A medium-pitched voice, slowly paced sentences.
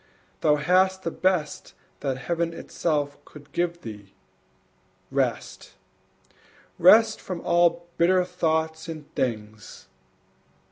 Yes: medium, 165 Hz; slow, 100 wpm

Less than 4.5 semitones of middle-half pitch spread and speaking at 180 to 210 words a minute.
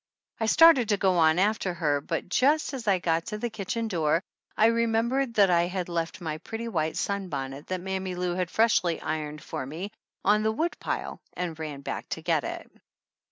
No: average, 5.2 semitones; average, 195 wpm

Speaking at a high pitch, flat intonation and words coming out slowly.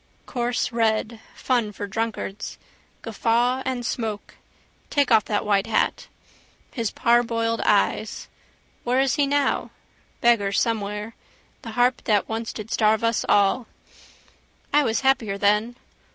Yes: high, 230 Hz; narrow, 2.3 semitones; slow, 125 wpm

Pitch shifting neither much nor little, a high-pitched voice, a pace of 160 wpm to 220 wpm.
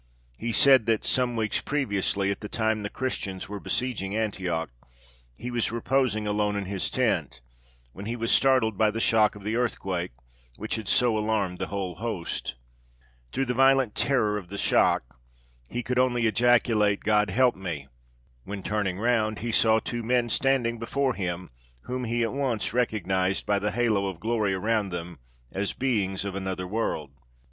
No: average, 3.5 semitones; low, 110 Hz; average, 170 wpm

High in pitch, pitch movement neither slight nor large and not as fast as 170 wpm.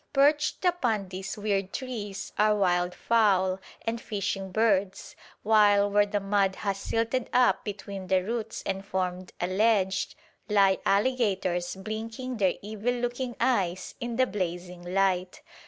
Yes: high, 200 Hz; average, 3.2 semitones; average, 140 wpm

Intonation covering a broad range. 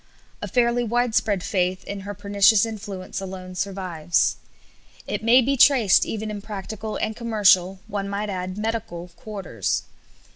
No: average, 3.0 semitones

